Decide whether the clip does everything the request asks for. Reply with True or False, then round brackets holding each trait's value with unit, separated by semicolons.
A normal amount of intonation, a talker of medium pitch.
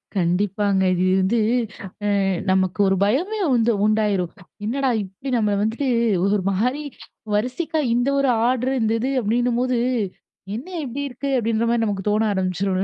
False (4.1 semitones; 220 Hz)